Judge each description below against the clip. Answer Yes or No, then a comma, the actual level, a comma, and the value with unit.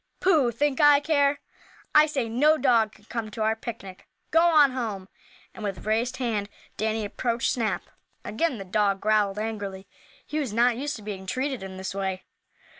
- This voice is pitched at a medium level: No, high, 225 Hz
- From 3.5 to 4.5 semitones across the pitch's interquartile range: No, average, 5.1 semitones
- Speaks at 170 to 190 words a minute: Yes, average, 180 wpm